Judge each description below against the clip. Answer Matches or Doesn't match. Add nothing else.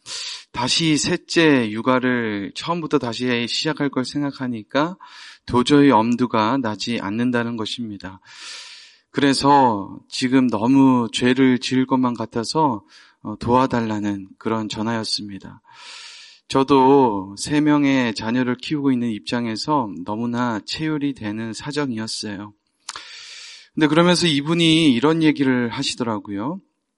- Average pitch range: Matches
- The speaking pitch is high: Doesn't match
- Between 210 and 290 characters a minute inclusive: Matches